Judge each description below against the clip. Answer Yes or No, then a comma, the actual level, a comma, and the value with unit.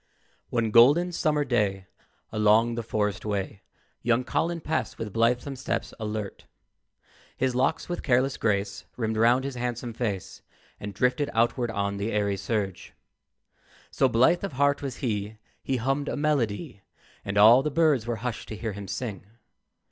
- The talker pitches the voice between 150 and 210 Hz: No, low, 115 Hz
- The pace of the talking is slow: No, average, 155 wpm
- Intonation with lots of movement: No, average, 4.1 semitones